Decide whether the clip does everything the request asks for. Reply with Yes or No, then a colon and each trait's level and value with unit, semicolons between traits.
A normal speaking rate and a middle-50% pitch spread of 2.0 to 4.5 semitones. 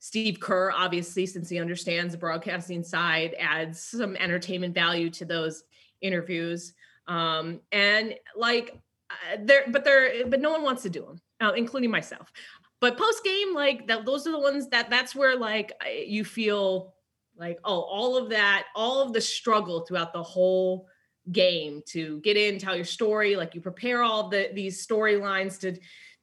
No: average, 170 wpm; average, 5.2 semitones